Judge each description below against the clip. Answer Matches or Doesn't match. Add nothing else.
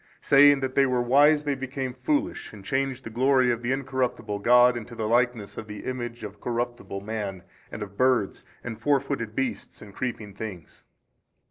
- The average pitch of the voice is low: Matches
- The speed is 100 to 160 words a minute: Doesn't match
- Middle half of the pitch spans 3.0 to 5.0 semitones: Matches